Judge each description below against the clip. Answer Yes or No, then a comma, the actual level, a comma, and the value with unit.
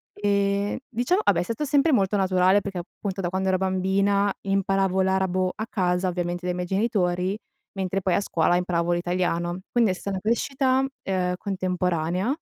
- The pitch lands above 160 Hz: Yes, high, 190 Hz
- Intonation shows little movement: Yes, narrow, 2.0 semitones